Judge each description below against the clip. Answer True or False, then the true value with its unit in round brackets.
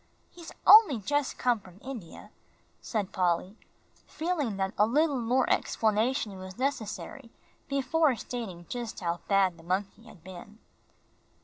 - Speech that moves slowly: True (130 wpm)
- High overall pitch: True (220 Hz)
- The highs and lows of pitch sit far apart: True (5.8 semitones)